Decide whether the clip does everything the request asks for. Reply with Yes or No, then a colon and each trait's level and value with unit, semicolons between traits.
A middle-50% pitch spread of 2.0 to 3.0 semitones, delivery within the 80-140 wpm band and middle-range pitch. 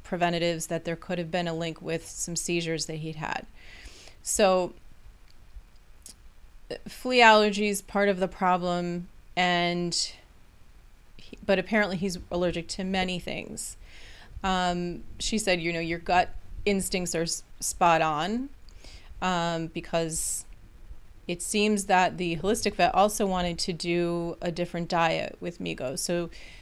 Yes: narrow, 2.4 semitones; slow, 135 wpm; medium, 175 Hz